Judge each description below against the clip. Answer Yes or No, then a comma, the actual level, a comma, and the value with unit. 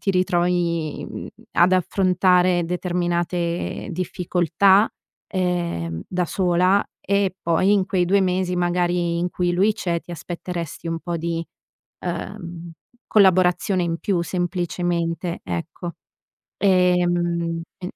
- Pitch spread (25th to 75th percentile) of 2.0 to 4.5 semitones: No, narrow, 1.3 semitones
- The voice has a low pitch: No, medium, 175 Hz